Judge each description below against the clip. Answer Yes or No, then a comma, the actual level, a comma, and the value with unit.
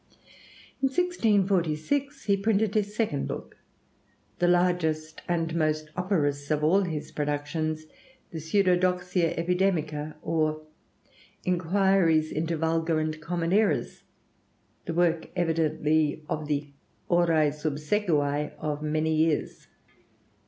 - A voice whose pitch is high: No, medium, 165 Hz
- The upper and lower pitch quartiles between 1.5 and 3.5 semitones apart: Yes, average, 2.9 semitones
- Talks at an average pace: No, slow, 105 wpm